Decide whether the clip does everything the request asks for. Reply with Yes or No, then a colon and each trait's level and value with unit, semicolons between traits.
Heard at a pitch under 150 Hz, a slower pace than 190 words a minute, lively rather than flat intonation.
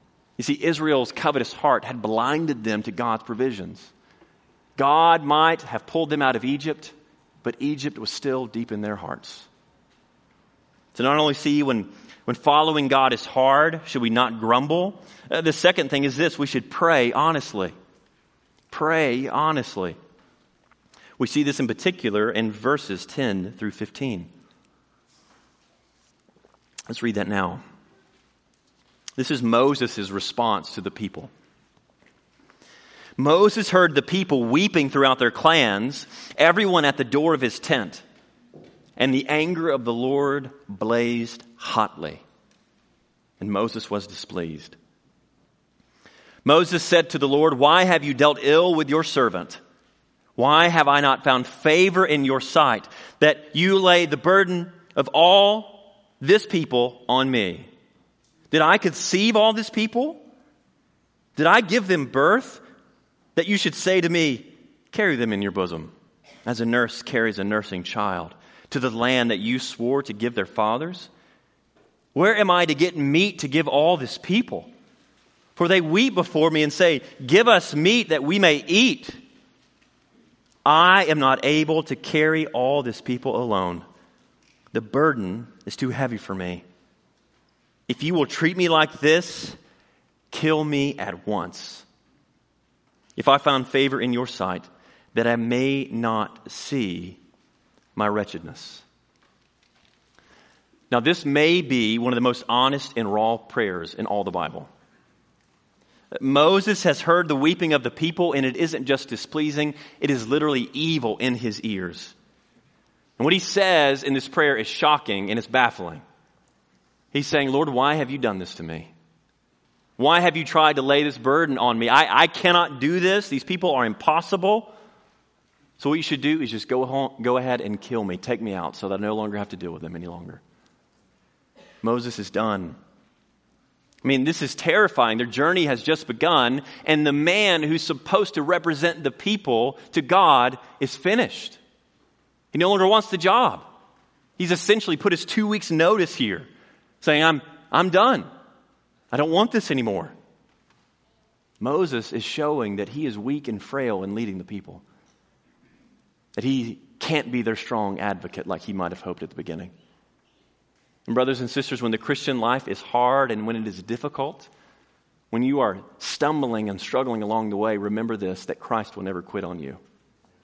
Yes: medium, 140 Hz; average, 160 wpm; wide, 6.1 semitones